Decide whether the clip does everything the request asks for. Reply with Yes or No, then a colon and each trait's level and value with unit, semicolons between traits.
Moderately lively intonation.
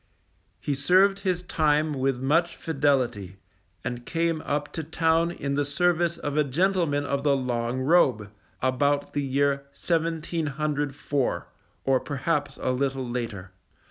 Yes: average, 3.5 semitones